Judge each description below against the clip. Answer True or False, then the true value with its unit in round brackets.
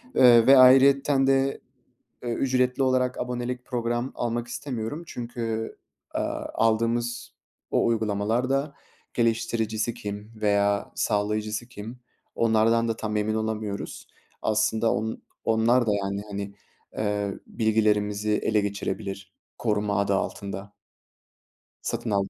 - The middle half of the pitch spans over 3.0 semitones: False (2.7 semitones)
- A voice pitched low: True (110 Hz)